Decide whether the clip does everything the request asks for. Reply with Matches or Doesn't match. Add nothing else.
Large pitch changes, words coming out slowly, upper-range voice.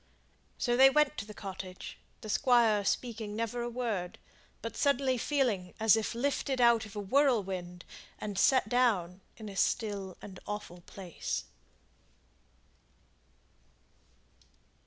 Doesn't match